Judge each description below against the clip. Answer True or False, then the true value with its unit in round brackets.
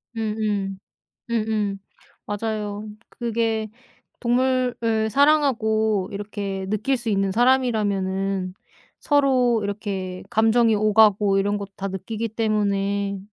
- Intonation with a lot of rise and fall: False (2.4 semitones)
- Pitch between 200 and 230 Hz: True (215 Hz)